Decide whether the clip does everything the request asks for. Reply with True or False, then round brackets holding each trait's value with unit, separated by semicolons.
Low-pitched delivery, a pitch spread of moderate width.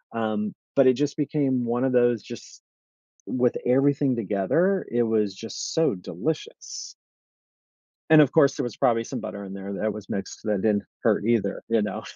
True (115 Hz; 4.4 semitones)